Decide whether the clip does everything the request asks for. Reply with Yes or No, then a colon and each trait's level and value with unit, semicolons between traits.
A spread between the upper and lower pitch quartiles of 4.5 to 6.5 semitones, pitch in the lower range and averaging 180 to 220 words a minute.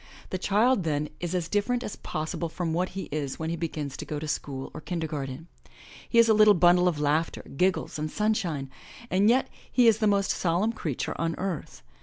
No: average, 4.9 semitones; medium, 175 Hz; fast, 205 wpm